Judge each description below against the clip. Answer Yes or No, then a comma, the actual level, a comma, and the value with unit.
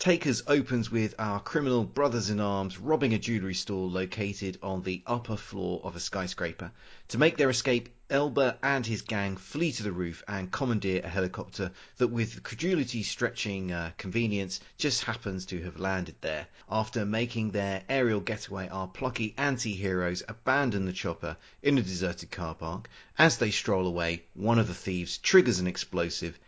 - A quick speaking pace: No, average, 170 wpm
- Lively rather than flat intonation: No, average, 4.5 semitones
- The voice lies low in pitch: Yes, low, 105 Hz